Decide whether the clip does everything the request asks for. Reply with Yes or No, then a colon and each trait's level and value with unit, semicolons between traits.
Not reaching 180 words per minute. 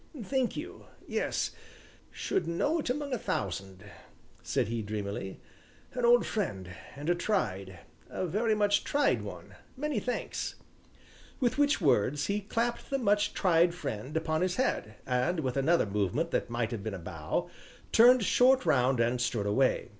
Yes: average, 160 wpm